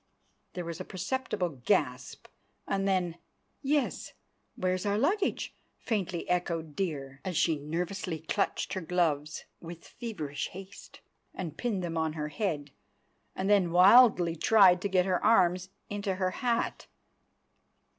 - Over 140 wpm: No, slow, 135 wpm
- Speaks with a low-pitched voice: No, medium, 180 Hz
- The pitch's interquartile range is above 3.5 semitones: No, average, 3.2 semitones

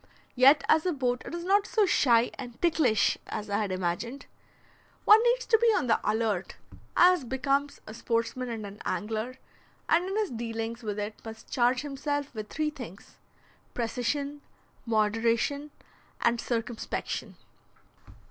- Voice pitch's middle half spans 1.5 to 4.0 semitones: No, average, 4.6 semitones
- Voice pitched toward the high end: Yes, high, 245 Hz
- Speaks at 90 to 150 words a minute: Yes, average, 145 wpm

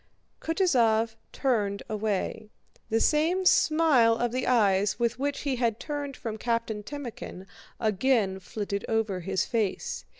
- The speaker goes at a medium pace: No, slow, 130 wpm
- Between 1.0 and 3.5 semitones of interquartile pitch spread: No, average, 4.2 semitones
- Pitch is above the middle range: Yes, high, 230 Hz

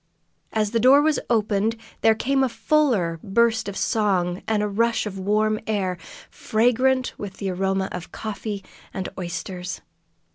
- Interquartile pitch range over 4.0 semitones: No, average, 3.3 semitones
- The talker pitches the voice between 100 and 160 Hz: No, high, 210 Hz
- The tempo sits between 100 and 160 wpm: Yes, average, 150 wpm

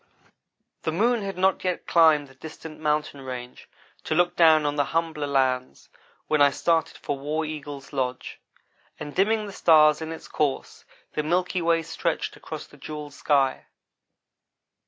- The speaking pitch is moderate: Yes, medium, 155 Hz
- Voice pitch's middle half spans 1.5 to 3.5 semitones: Yes, narrow, 2.6 semitones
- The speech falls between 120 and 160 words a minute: Yes, average, 155 wpm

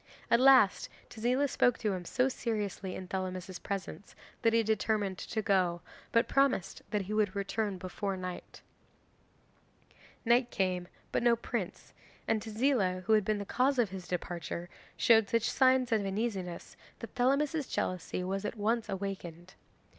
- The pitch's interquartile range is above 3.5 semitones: Yes, average, 3.9 semitones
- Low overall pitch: No, high, 205 Hz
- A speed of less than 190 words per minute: Yes, average, 155 wpm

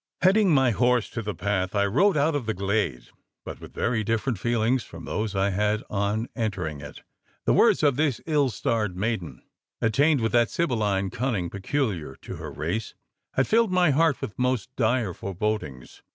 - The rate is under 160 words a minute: No, average, 180 wpm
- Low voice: Yes, low, 110 Hz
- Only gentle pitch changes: No, average, 5.0 semitones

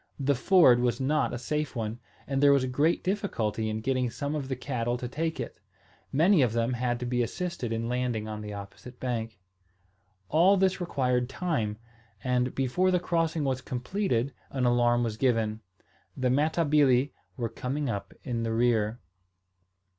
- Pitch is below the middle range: Yes, low, 125 Hz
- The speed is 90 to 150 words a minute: No, average, 170 wpm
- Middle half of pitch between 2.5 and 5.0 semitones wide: Yes, average, 4.0 semitones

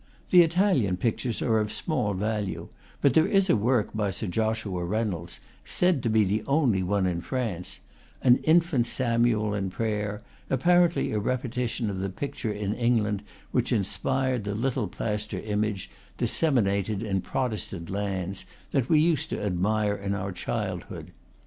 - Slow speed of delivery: No, average, 160 wpm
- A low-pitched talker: Yes, low, 110 Hz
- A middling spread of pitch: Yes, average, 4.2 semitones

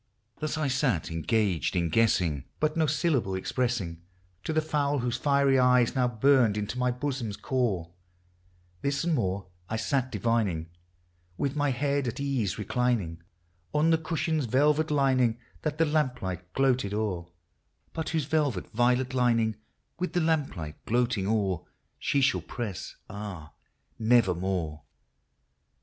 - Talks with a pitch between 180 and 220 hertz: No, low, 125 Hz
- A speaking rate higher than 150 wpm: No, average, 140 wpm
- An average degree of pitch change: No, wide, 5.9 semitones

